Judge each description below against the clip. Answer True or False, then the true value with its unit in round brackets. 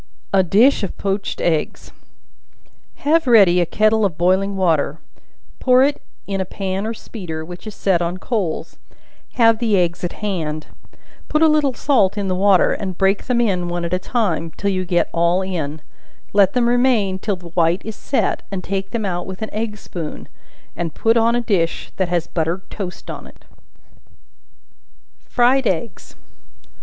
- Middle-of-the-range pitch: False (195 Hz)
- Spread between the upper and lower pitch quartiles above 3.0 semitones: True (4.1 semitones)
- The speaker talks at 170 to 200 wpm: True (175 wpm)